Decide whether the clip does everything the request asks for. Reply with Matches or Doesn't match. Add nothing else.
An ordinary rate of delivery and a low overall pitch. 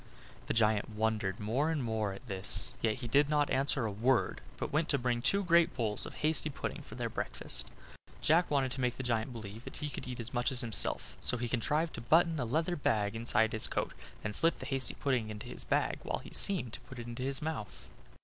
Doesn't match